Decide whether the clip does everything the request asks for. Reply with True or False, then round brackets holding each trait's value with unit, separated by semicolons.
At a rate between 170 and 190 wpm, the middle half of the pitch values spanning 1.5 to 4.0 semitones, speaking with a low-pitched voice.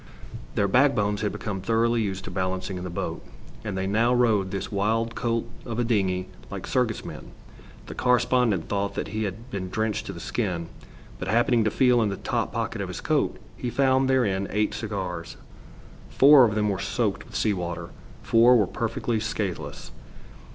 True (185 wpm; 3.6 semitones; 105 Hz)